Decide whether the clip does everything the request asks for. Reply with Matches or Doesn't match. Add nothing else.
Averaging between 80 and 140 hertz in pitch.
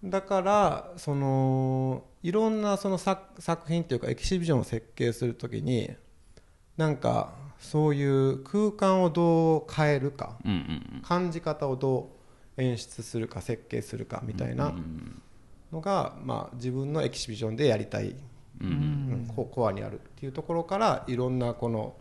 Matches